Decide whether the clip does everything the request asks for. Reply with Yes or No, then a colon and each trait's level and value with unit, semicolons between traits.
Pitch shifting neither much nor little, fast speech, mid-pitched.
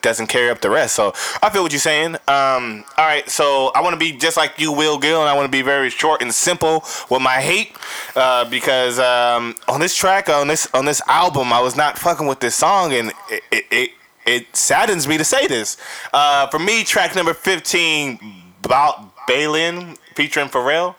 Yes: average, 4.4 semitones; fast, 215 wpm; medium, 150 Hz